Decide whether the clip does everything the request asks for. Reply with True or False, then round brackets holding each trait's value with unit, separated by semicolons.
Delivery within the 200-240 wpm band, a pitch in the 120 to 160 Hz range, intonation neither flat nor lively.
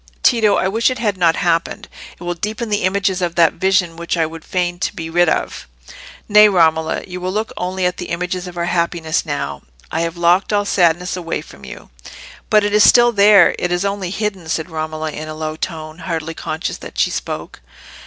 False (205 wpm; 175 Hz; 3.3 semitones)